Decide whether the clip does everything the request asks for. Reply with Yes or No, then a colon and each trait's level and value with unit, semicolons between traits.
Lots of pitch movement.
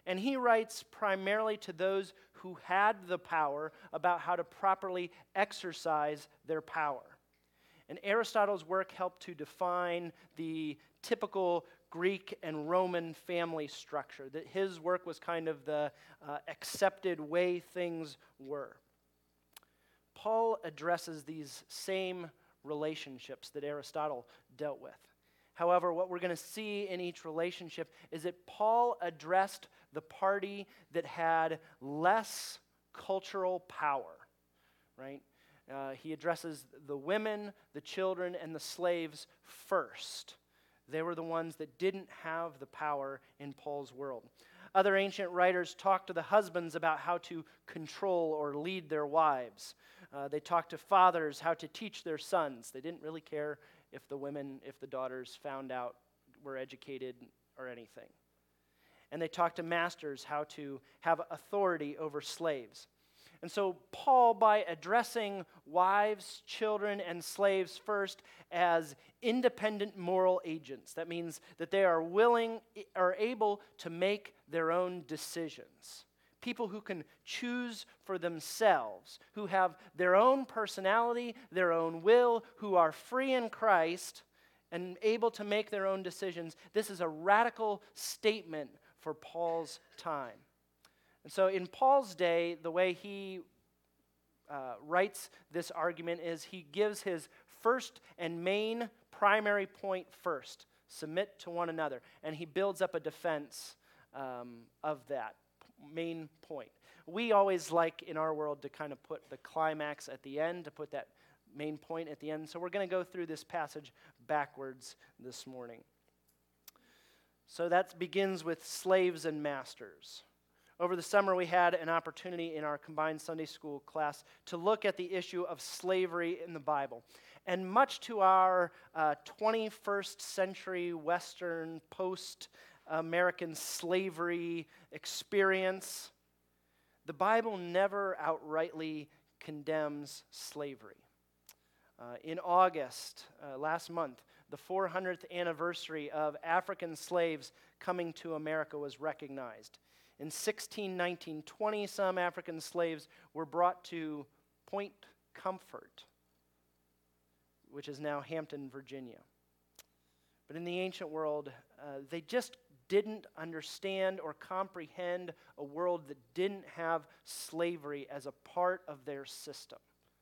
No: average, 4.1 semitones